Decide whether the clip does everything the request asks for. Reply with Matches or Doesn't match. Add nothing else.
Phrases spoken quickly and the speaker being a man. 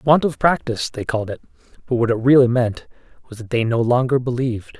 Matches